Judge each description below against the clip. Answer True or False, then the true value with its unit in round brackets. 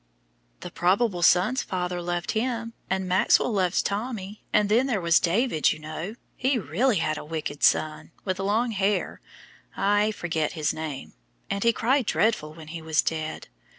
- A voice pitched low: False (190 Hz)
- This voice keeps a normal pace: True (165 wpm)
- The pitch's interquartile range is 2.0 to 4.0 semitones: False (5.2 semitones)